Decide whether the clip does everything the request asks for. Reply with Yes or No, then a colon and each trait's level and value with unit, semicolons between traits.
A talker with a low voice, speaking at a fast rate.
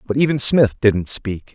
No: low, 115 Hz; average, 195 wpm